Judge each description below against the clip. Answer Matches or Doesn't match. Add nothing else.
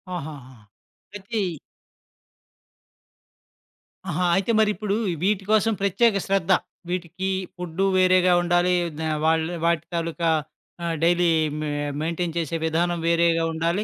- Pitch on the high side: Doesn't match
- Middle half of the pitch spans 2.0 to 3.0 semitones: Matches